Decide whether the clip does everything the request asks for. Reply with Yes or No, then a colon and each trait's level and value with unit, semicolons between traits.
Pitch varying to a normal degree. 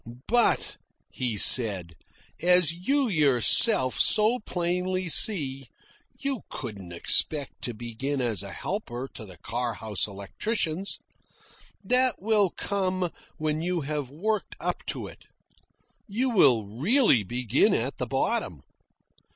No: wide, 9.0 semitones